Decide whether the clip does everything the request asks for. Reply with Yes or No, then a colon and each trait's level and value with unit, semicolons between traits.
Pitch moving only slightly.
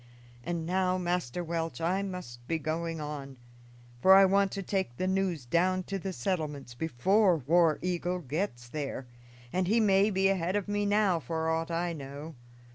No: average, 3.4 semitones